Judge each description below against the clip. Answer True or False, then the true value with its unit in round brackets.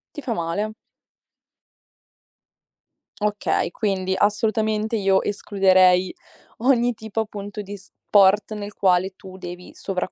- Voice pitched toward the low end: False (205 Hz)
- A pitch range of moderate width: False (2.3 semitones)